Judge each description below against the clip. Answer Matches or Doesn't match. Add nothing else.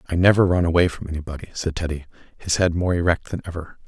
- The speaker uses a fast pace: Matches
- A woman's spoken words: Doesn't match